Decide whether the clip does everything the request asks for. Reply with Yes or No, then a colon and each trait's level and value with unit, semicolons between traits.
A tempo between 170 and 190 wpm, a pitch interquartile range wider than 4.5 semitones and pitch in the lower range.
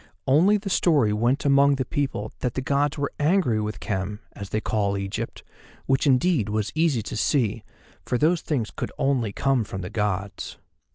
Yes: average, 180 wpm; average, 5.3 semitones; low, 125 Hz